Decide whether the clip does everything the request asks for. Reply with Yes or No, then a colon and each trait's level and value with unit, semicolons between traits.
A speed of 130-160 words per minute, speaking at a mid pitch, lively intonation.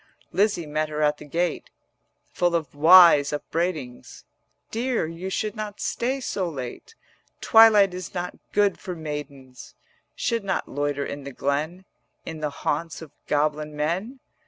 No: average, 150 wpm; medium, 165 Hz; average, 4.4 semitones